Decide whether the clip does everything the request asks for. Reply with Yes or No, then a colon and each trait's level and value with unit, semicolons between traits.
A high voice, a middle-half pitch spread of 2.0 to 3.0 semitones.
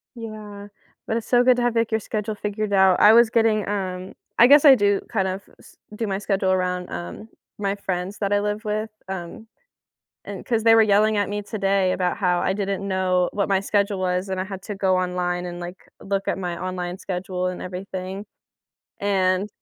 Yes: high, 195 Hz; narrow, 2.4 semitones